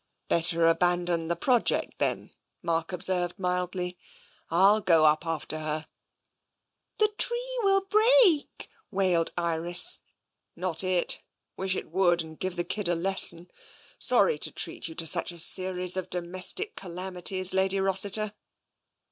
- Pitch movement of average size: No, narrow, 2.3 semitones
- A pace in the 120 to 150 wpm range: Yes, average, 145 wpm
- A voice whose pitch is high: No, medium, 180 Hz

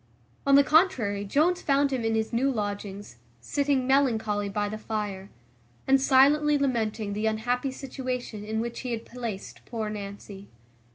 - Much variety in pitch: No, average, 4.5 semitones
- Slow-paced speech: No, average, 155 wpm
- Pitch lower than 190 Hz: No, high, 230 Hz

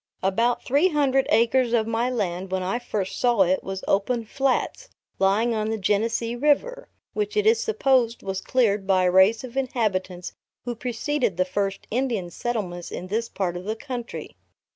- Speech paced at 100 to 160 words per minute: No, average, 175 wpm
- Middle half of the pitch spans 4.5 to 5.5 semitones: Yes, average, 4.8 semitones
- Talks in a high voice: Yes, high, 230 Hz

